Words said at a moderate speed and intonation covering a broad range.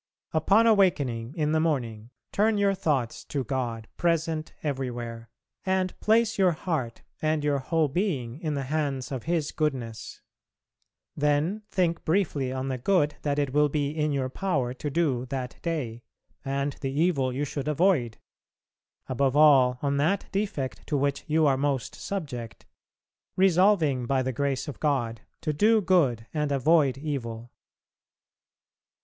No: average, 150 wpm; average, 4.0 semitones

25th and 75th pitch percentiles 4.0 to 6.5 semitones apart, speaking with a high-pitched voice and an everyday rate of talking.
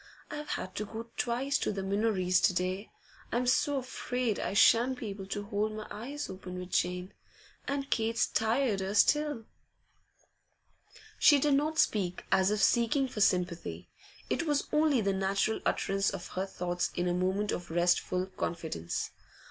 Yes: average, 5.1 semitones; high, 210 Hz; average, 160 wpm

